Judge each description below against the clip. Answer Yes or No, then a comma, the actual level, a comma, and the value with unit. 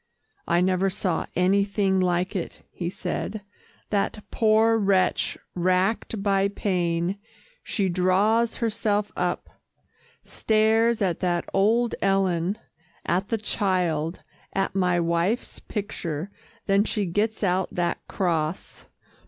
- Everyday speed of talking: No, slow, 110 wpm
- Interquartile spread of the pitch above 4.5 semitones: No, average, 2.8 semitones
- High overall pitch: Yes, high, 195 Hz